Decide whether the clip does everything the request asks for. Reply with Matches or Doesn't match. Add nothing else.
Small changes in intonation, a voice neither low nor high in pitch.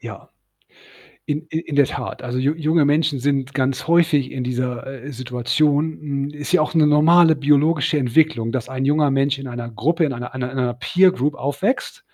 Doesn't match